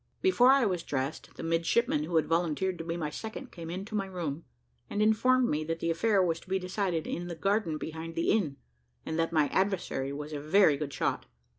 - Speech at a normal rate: No, fast, 215 wpm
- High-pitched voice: No, medium, 170 Hz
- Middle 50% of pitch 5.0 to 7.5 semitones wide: No, average, 4.1 semitones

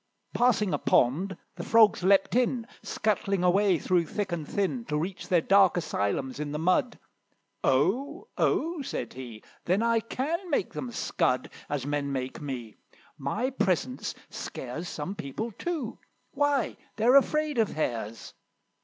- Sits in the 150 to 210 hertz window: Yes, high, 190 Hz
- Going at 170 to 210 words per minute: No, average, 145 wpm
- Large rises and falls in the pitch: Yes, wide, 8.2 semitones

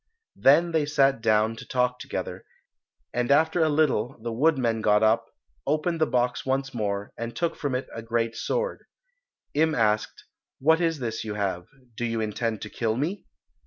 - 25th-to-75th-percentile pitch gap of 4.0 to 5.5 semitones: Yes, average, 5.2 semitones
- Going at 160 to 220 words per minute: Yes, average, 175 wpm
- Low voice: Yes, low, 125 Hz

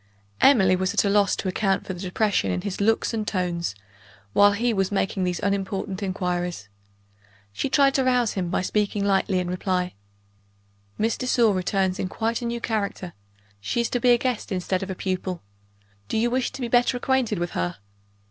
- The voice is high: Yes, high, 200 Hz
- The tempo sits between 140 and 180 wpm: No, average, 195 wpm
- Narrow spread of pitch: No, average, 3.9 semitones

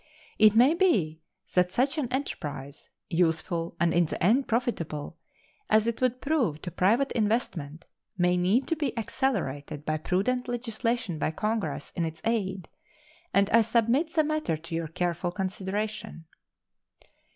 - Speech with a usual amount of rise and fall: No, wide, 6.6 semitones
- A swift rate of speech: No, average, 145 wpm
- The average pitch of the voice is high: Yes, high, 200 Hz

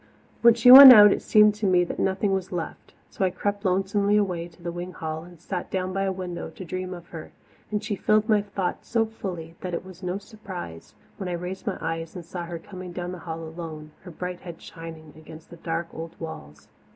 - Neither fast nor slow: No, fast, 230 wpm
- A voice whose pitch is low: No, medium, 180 Hz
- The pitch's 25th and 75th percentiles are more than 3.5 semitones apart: No, average, 3.0 semitones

